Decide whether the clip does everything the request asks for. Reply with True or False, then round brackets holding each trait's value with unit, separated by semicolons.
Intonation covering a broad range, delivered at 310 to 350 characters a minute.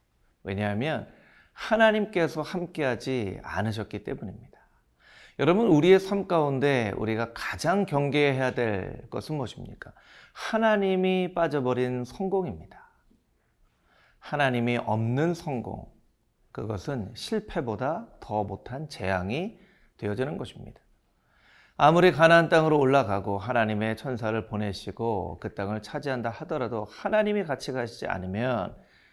False (7.0 semitones; 285 characters per minute)